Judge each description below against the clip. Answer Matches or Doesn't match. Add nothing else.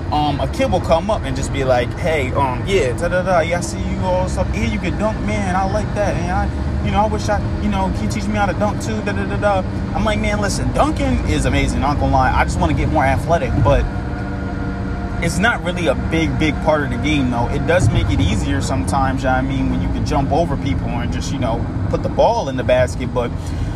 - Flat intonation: Matches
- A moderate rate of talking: Doesn't match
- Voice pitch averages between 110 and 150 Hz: Doesn't match